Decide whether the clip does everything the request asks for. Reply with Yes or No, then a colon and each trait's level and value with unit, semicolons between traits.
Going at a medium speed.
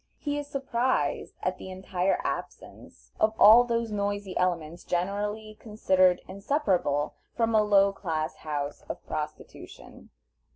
No: slow, 125 wpm